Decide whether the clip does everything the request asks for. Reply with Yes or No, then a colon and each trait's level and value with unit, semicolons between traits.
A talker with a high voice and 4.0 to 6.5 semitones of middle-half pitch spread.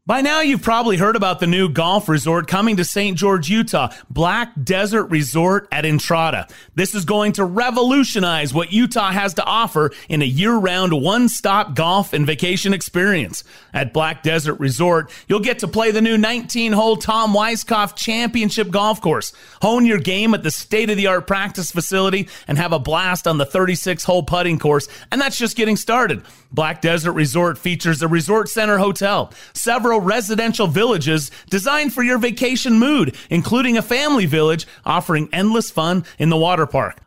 Yes: high, 195 Hz; average, 5.0 semitones